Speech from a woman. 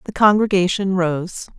Yes: female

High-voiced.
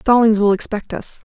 Yes: high, 215 Hz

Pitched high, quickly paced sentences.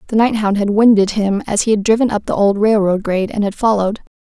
Yes: high, 210 Hz; fast, 240 wpm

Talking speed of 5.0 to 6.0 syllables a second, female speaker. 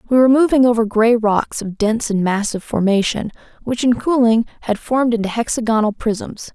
Yes: 5.7 syllables/s; female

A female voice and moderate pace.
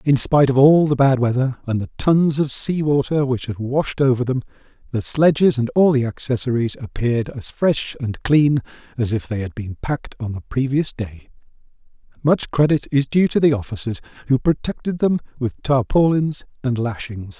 No: male; average, 180 wpm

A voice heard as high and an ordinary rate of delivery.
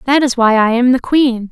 No: high, 245 Hz; fast, 280 wpm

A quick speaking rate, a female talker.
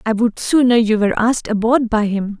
Yes: fast, 225 wpm; female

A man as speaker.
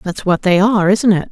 No: female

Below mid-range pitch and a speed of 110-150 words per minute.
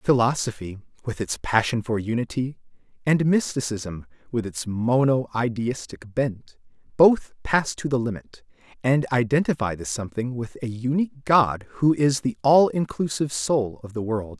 Yes: low, 125 Hz; average, 140 wpm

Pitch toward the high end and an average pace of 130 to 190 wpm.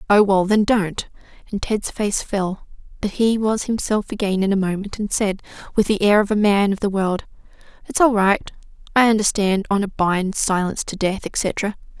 Yes: high, 200 Hz; average, 175 wpm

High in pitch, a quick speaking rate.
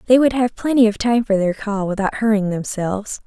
Yes: high, 215 Hz; fast, 220 wpm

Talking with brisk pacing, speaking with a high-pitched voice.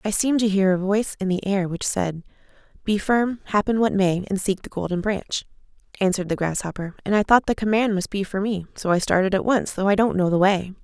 Yes: fast, 245 wpm; high, 195 Hz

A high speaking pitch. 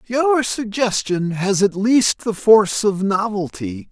Yes: high, 205 Hz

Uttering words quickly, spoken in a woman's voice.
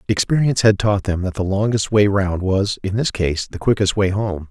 No: fast, 225 wpm; male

